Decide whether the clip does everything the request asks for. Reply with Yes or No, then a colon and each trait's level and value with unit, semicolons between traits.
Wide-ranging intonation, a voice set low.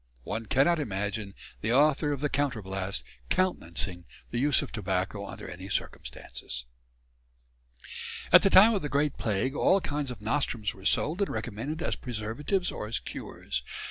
Yes: wide, 6.7 semitones; low, 120 Hz